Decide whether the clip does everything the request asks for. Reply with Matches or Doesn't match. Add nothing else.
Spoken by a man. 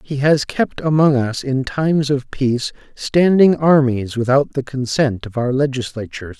Matches